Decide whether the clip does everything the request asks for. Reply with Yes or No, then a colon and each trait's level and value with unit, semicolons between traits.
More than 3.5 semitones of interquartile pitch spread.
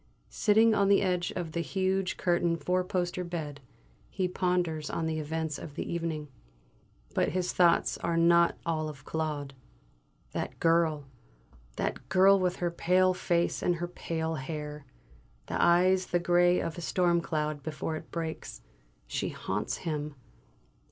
No: narrow, 2.4 semitones